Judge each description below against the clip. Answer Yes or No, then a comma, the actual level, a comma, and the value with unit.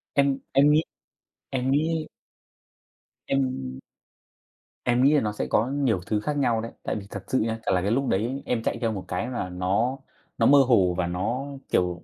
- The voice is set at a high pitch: No, low, 120 Hz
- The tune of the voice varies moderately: No, wide, 5.8 semitones